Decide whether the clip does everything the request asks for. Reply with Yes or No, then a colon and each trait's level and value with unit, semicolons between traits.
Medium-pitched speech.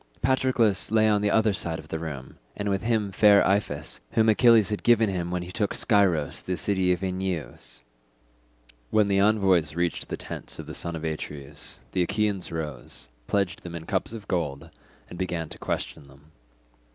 No: very low, 95 Hz